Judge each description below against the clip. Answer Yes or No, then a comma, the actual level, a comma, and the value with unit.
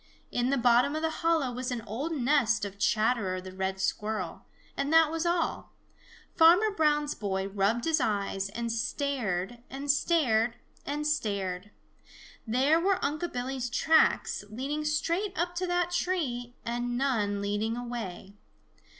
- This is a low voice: No, high, 245 Hz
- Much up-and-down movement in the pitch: Yes, wide, 6.2 semitones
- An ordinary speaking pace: Yes, average, 145 wpm